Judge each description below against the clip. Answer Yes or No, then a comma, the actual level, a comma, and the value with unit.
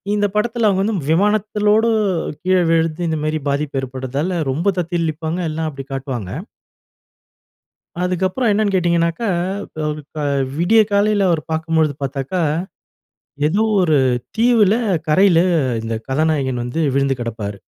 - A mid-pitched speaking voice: Yes, medium, 165 Hz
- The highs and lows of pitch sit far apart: Yes, wide, 5.9 semitones